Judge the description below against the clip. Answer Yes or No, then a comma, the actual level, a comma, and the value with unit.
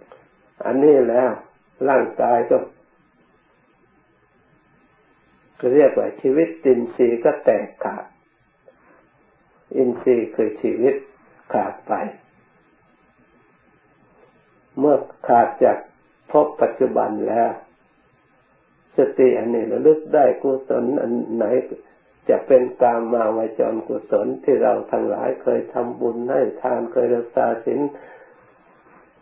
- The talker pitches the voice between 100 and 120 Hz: No, low, 135 Hz